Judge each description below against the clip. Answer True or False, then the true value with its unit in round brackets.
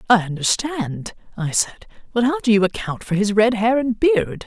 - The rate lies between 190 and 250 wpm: True (200 wpm)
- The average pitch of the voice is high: True (220 Hz)